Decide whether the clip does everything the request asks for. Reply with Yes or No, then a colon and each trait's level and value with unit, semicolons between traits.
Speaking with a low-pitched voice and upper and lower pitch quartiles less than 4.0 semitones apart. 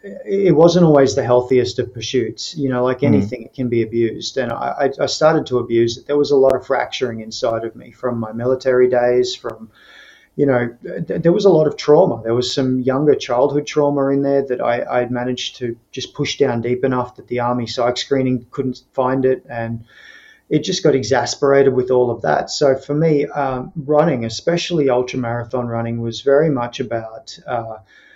Yes: low, 125 Hz; average, 2.7 semitones